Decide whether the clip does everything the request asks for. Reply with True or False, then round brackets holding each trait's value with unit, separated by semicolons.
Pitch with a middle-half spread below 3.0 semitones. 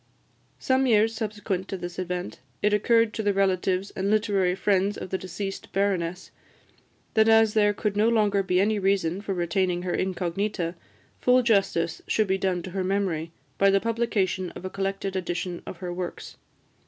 True (2.4 semitones)